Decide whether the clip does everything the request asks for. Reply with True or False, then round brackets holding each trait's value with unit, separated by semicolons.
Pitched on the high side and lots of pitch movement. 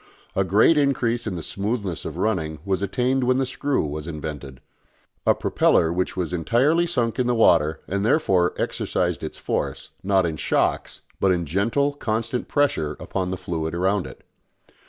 False (100 Hz; 6.4 semitones)